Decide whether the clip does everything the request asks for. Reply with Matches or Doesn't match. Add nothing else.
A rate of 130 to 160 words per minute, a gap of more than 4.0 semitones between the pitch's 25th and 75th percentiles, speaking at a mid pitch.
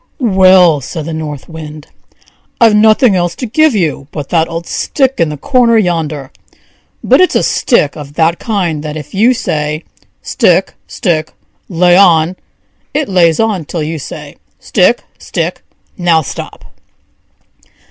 Matches